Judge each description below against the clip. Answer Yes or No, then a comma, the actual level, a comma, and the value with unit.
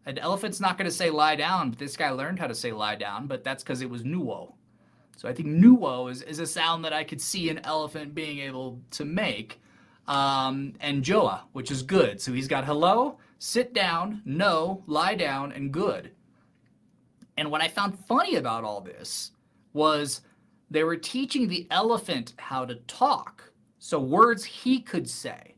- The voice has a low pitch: No, medium, 155 Hz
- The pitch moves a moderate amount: No, wide, 6.0 semitones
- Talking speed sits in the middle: Yes, average, 185 wpm